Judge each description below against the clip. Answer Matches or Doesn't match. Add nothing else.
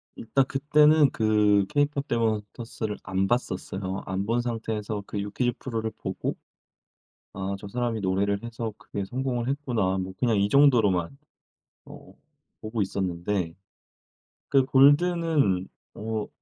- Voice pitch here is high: Doesn't match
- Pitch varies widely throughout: Doesn't match